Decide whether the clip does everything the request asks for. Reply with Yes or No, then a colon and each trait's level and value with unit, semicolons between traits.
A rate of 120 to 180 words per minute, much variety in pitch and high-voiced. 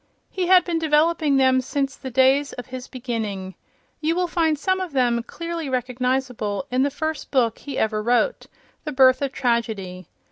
No: average, 175 wpm; average, 4.3 semitones; very high, 265 Hz